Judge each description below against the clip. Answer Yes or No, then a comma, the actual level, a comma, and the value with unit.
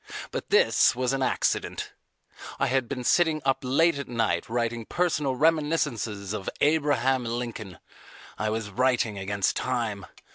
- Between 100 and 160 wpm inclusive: Yes, average, 140 wpm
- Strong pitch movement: No, average, 4.1 semitones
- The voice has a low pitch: Yes, low, 125 Hz